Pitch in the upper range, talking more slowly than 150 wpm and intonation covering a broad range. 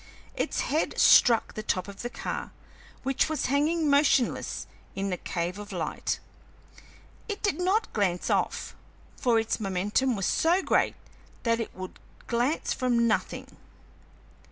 Yes: high, 235 Hz; average, 140 wpm; wide, 6.4 semitones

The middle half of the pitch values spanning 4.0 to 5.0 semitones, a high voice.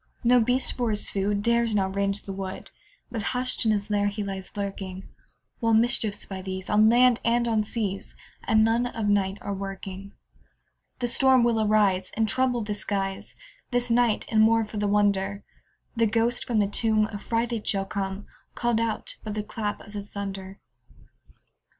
No: average, 2.7 semitones; high, 210 Hz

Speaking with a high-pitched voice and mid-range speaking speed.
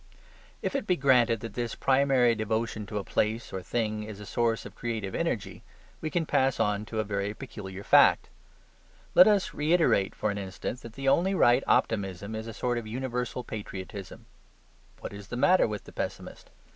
No: low, 115 Hz; average, 185 wpm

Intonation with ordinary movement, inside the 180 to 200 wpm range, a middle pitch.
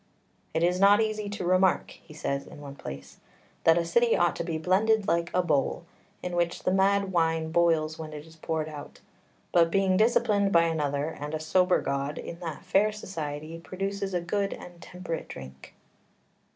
Yes: average, 3.6 semitones; average, 185 wpm; medium, 170 Hz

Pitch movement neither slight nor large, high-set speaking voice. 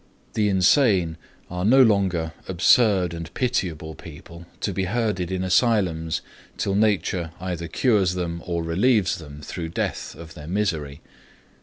No: average, 3.7 semitones; very low, 90 Hz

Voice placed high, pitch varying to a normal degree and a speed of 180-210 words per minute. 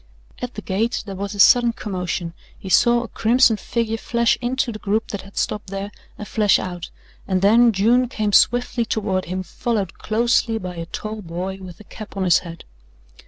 Yes: high, 210 Hz; average, 3.7 semitones; average, 195 wpm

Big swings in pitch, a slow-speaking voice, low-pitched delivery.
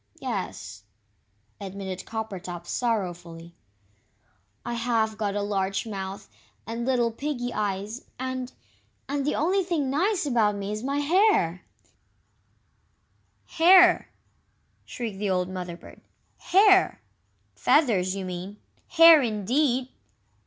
No: wide, 6.4 semitones; slow, 110 wpm; high, 220 Hz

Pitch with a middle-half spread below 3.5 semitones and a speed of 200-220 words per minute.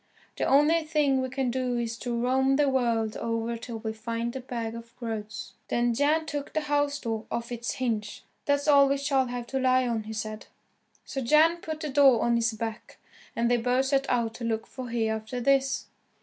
Yes: average, 3.1 semitones; fast, 205 wpm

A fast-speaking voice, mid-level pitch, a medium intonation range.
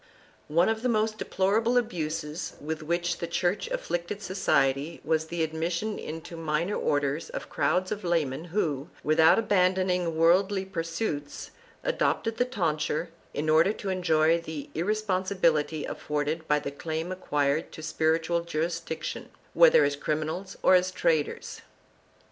No: average, 145 wpm; medium, 170 Hz; average, 3.3 semitones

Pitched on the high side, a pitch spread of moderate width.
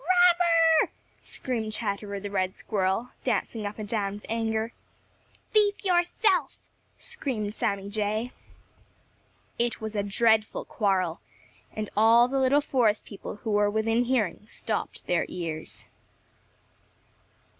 Yes: high, 220 Hz; average, 4.1 semitones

